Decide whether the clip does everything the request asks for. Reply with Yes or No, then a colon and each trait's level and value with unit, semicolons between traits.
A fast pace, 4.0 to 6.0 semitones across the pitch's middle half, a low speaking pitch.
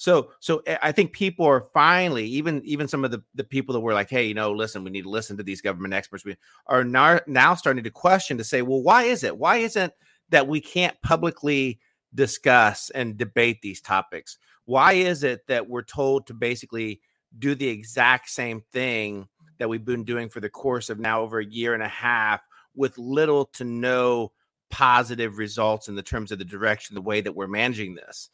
Yes: fast, 210 wpm; average, 4.4 semitones; low, 120 Hz